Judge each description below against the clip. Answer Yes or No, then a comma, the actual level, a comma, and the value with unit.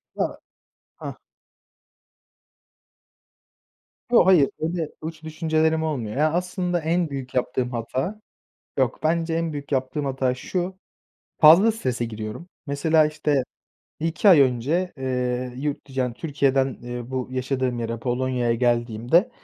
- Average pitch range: Yes, average, 4.5 semitones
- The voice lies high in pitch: No, medium, 140 Hz